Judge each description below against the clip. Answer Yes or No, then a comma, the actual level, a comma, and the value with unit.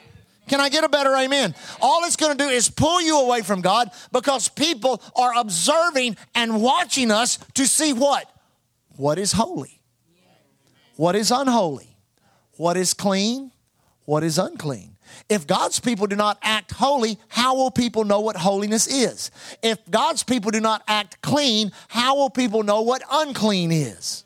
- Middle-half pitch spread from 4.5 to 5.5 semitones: Yes, average, 4.8 semitones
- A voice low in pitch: No, high, 230 Hz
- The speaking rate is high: No, average, 165 wpm